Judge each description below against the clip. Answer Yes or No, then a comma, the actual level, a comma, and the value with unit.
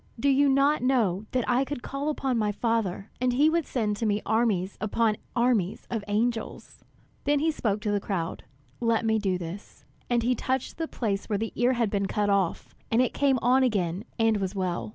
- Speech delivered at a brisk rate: Yes, fast, 210 wpm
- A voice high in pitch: Yes, high, 225 Hz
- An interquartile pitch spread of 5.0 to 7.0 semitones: No, average, 3.9 semitones